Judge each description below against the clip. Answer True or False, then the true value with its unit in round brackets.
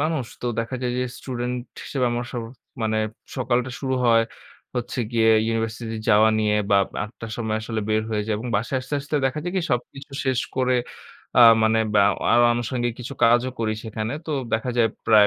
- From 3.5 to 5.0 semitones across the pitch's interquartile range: False (2.4 semitones)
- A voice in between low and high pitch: False (120 Hz)